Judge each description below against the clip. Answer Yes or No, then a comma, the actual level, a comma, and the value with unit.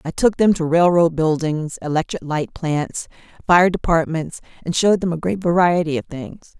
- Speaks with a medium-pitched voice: Yes, medium, 165 Hz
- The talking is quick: No, average, 175 wpm